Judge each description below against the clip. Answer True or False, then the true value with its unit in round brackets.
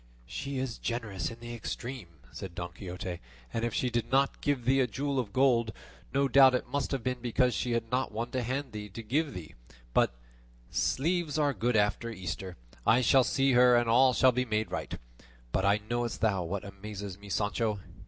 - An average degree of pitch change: True (3.8 semitones)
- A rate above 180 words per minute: True (200 wpm)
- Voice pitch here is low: True (120 Hz)